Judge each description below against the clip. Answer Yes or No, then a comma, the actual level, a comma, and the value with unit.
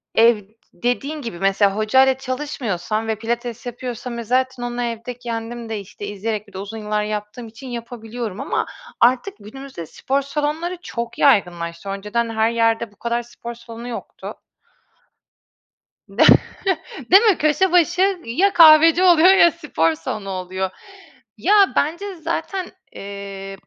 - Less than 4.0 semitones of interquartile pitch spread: No, average, 5.0 semitones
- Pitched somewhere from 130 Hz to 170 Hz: No, high, 235 Hz